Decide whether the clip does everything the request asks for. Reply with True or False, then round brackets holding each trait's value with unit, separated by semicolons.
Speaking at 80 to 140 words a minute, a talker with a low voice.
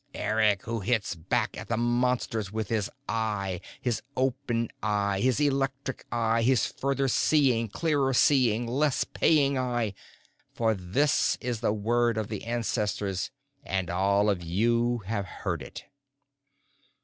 True (135 wpm; 115 Hz)